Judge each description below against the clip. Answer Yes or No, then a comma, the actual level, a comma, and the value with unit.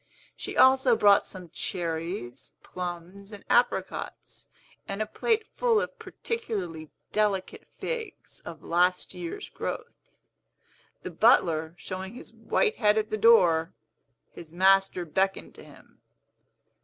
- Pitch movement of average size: Yes, average, 4.1 semitones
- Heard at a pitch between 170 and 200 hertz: Yes, high, 190 Hz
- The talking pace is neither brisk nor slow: No, slow, 120 wpm